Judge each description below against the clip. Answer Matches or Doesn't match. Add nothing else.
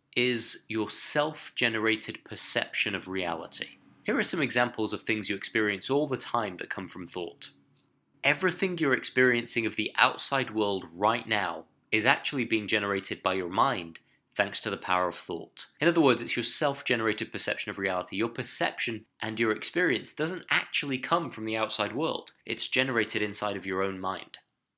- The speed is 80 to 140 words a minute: Doesn't match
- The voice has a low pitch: Matches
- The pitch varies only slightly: Doesn't match